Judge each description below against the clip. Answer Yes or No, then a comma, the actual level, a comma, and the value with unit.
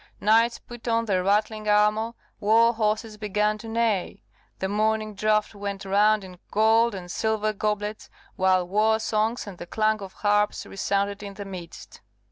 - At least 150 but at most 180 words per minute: Yes, average, 160 wpm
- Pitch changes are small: Yes, narrow, 1.5 semitones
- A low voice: No, high, 210 Hz